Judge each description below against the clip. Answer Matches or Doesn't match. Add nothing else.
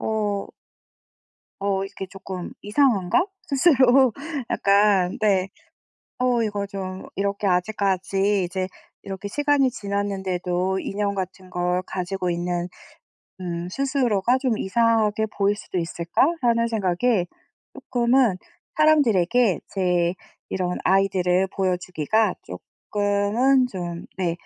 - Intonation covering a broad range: Doesn't match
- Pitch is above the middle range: Matches